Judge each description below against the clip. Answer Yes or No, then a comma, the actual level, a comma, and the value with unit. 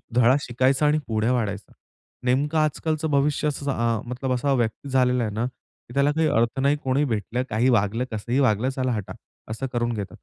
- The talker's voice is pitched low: Yes, low, 125 Hz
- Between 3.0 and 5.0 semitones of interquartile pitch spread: Yes, average, 3.3 semitones